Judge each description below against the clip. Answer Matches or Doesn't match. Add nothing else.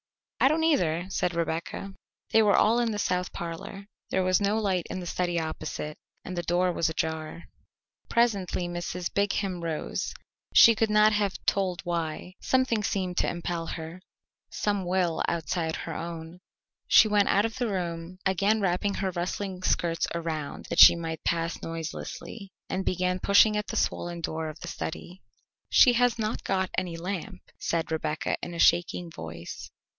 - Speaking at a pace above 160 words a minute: Matches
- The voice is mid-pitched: Matches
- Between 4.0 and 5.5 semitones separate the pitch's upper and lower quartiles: Doesn't match